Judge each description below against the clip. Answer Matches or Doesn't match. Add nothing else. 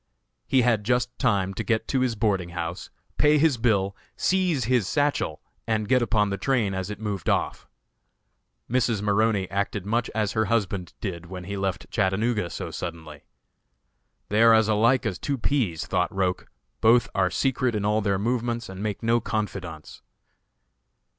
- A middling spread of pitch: Matches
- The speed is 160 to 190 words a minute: Matches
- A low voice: Matches